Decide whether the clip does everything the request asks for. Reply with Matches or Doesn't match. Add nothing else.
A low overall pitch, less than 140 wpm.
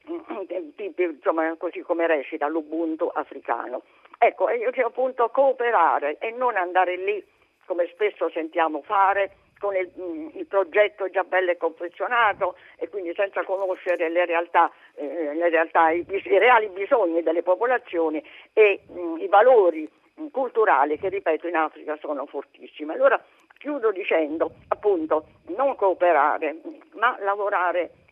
Doesn't match